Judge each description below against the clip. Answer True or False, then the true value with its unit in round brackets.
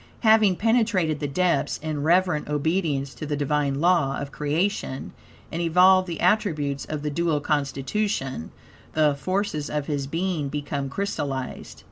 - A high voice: False (155 Hz)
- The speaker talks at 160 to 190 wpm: False (140 wpm)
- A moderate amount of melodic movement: True (4.3 semitones)